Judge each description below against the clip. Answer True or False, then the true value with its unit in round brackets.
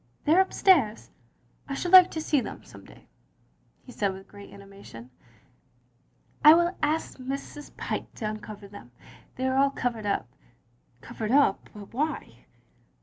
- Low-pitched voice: False (245 Hz)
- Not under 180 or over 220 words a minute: False (170 wpm)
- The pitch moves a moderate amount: False (6.8 semitones)